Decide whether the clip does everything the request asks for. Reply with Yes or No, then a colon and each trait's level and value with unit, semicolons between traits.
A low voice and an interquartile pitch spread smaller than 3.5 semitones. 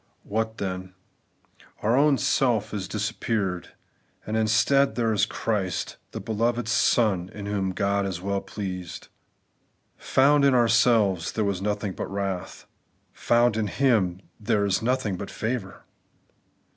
Yes: low, 105 Hz; average, 3.0 semitones